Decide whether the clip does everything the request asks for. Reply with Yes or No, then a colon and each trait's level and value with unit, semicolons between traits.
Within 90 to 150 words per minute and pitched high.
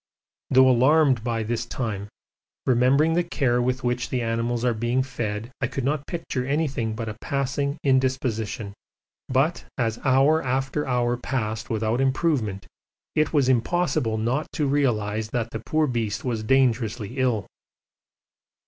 No: average, 145 wpm; low, 125 Hz